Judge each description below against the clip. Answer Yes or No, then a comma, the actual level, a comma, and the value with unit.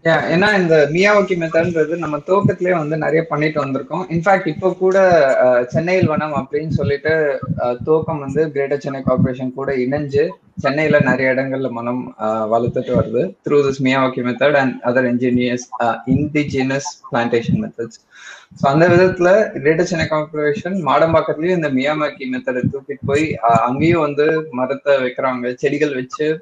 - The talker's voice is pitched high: No, medium, 145 Hz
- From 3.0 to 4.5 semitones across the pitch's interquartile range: Yes, average, 3.8 semitones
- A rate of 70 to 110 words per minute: No, fast, 130 wpm